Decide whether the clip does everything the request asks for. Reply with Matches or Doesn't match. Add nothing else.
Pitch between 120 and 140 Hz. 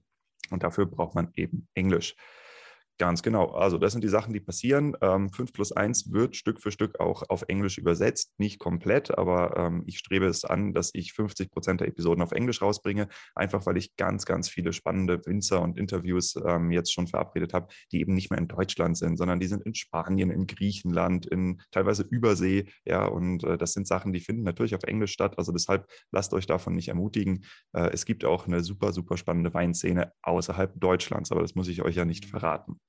Doesn't match